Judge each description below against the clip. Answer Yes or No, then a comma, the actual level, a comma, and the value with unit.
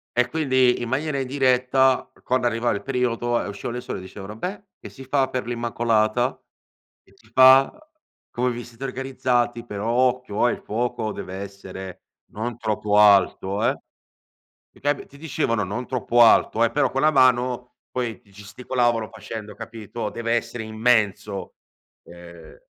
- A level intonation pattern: No, average, 3.0 semitones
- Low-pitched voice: Yes, low, 120 Hz